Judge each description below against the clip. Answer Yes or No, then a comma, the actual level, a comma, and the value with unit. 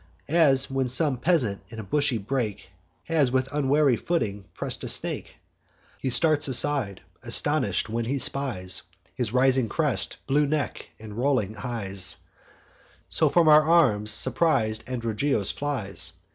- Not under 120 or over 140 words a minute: Yes, slow, 135 wpm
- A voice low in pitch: Yes, low, 130 Hz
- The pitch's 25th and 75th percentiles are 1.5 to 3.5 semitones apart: No, average, 5.1 semitones